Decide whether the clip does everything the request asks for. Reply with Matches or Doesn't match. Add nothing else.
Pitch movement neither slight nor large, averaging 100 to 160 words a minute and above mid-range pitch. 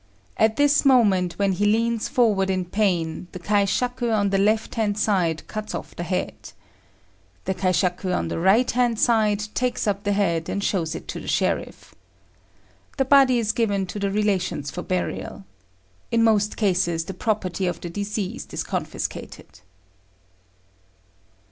Matches